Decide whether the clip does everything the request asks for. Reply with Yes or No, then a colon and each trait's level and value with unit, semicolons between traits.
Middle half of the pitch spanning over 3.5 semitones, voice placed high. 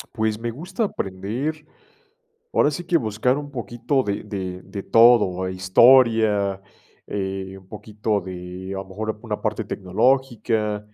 No: average, 4.1 semitones; low, 105 Hz